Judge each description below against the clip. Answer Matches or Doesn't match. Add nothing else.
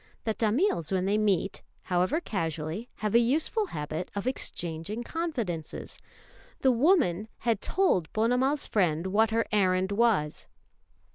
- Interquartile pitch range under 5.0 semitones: Doesn't match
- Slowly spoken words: Matches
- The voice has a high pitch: Matches